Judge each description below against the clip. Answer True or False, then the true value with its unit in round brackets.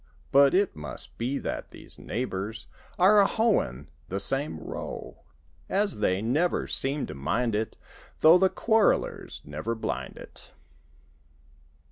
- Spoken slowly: True (130 wpm)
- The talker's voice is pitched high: False (130 Hz)